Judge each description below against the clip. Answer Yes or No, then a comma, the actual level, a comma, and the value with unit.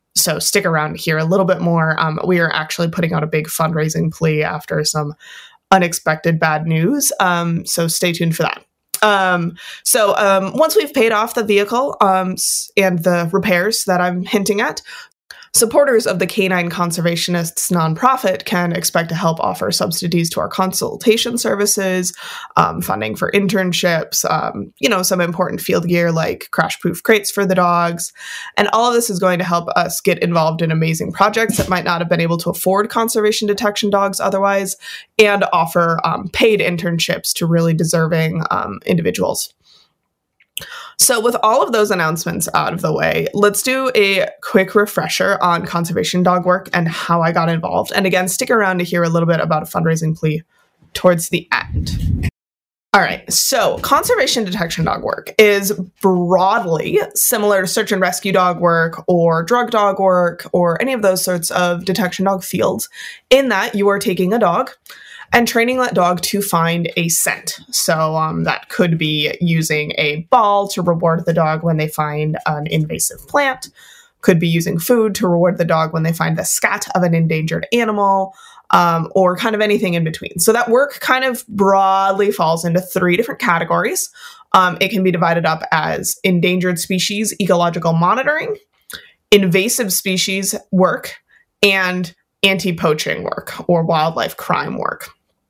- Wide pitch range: No, average, 3.3 semitones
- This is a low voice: No, medium, 185 Hz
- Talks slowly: No, average, 175 wpm